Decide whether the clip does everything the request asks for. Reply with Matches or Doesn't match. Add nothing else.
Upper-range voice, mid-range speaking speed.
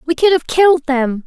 Doesn't match